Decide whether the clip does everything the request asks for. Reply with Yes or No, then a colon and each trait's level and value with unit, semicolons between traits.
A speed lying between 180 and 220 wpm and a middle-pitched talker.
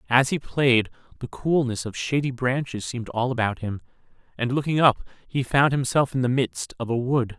No: average, 195 wpm; low, 125 Hz